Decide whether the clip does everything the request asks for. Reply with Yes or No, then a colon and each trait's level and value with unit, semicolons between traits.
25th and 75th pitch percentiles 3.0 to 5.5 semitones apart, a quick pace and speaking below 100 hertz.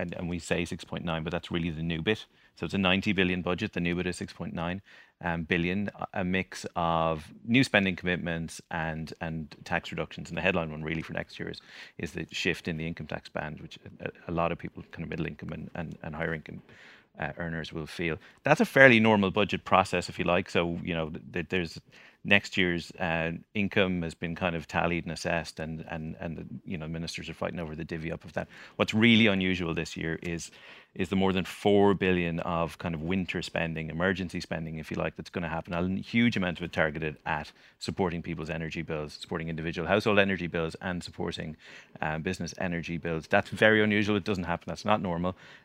No: narrow, 2.6 semitones; fast, 220 wpm; very low, 85 Hz